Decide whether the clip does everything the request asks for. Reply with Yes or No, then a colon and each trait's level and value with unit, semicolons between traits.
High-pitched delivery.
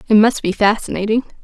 Yes: high, 215 Hz